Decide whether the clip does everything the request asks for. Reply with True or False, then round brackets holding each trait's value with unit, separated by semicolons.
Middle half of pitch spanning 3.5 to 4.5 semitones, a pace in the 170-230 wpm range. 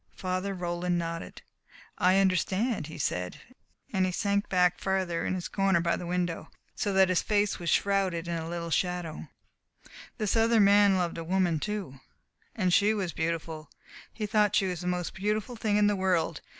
False (2.9 semitones; 180 wpm)